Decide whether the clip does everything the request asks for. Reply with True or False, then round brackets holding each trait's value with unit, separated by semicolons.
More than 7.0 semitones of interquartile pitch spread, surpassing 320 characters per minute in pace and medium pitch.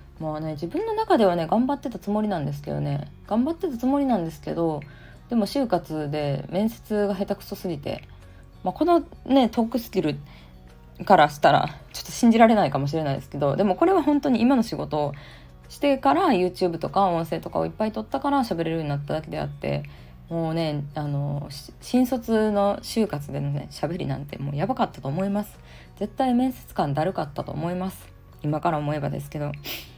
True (7.8 semitones; 400 characters per minute; 170 Hz)